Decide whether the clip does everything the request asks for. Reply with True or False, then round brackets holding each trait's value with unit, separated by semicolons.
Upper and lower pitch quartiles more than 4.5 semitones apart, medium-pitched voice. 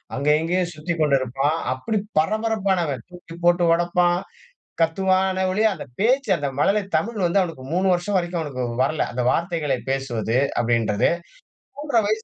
True (5.0 semitones; 175 Hz)